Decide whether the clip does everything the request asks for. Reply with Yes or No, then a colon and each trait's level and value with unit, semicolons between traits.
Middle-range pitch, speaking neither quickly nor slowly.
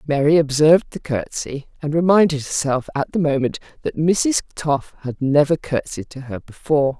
Yes: medium, 145 Hz; average, 165 wpm